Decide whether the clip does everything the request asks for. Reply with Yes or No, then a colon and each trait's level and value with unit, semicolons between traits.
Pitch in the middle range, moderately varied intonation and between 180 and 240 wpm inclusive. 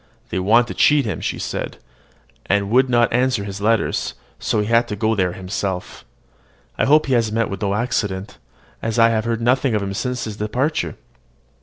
No: low, 110 Hz; average, 3.3 semitones; average, 190 wpm